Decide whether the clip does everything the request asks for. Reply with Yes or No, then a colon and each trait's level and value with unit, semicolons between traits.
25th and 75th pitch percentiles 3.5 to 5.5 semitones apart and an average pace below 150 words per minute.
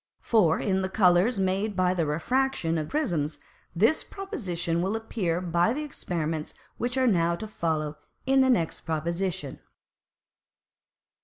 Yes: average, 5.2 semitones; average, 140 wpm